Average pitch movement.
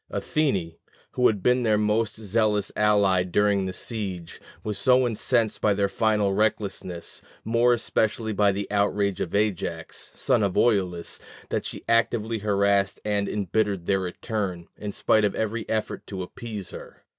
No: narrow, 2.2 semitones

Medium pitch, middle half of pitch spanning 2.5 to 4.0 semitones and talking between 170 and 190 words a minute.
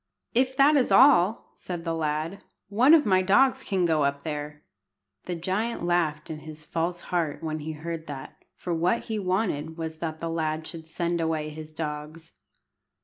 Yes: medium, 165 Hz; average, 3.1 semitones; average, 180 wpm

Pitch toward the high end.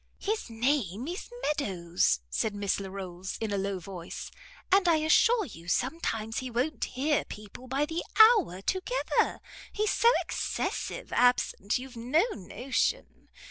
Yes: high, 245 Hz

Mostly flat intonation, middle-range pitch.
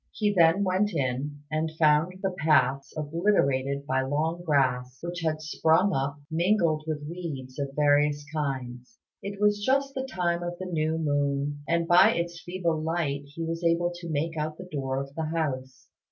No: average, 3.5 semitones; medium, 155 Hz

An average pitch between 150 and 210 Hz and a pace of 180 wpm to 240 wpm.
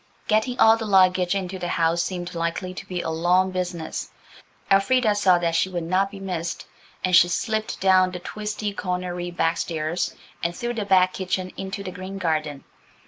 Yes: medium, 185 Hz; average, 185 wpm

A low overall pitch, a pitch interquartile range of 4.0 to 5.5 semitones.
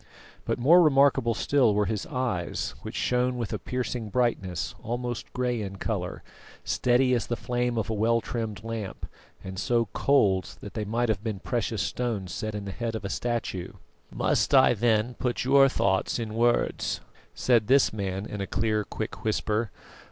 No: low, 115 Hz; average, 2.8 semitones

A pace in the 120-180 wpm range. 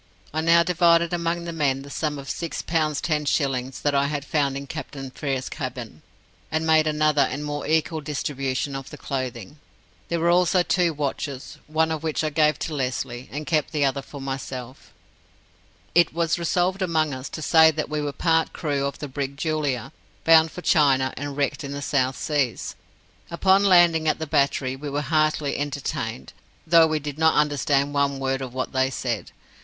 No: average, 190 wpm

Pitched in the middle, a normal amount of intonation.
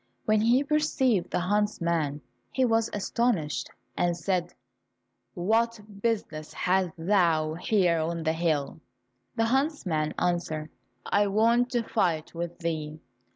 No: medium, 180 Hz; wide, 5.7 semitones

